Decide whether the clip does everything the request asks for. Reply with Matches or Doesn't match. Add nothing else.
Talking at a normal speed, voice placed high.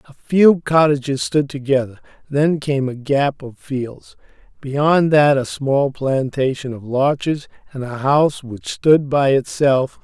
Doesn't match